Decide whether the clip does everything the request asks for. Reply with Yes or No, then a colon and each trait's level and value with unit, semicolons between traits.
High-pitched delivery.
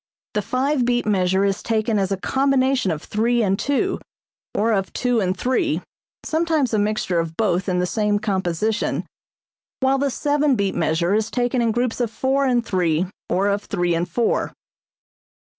Yes: high, 215 Hz